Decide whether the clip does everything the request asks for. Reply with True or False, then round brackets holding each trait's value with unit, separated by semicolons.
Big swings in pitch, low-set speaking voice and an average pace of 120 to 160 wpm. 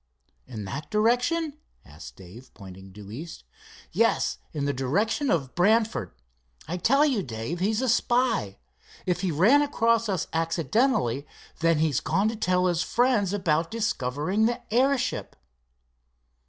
False (8.7 semitones; 180 Hz; 140 wpm)